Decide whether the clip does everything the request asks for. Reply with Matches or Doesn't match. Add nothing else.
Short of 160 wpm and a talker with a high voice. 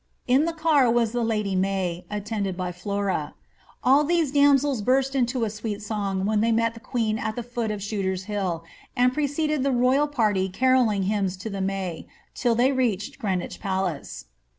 Doesn't match